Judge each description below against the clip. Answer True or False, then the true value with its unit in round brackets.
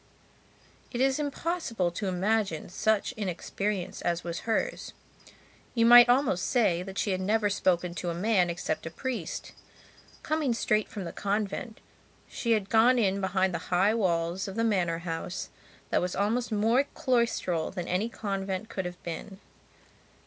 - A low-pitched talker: False (200 Hz)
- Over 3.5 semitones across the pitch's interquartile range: True (4.2 semitones)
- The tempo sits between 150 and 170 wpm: True (155 wpm)